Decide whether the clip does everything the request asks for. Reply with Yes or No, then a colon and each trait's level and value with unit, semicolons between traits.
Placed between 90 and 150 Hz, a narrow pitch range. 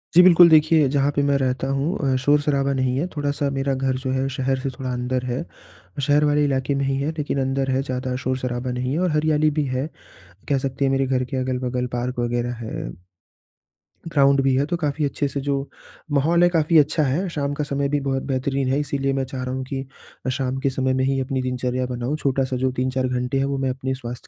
Yes: low, 135 Hz; narrow, 1.9 semitones